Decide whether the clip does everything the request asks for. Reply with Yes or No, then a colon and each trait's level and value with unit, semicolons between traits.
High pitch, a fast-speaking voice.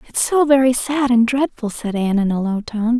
Yes: high, 240 Hz; fast, 240 wpm